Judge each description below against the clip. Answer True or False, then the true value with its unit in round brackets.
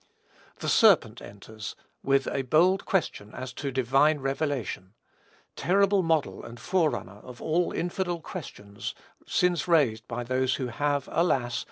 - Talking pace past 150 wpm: False (135 wpm)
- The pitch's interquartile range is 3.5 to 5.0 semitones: False (5.6 semitones)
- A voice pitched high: False (135 Hz)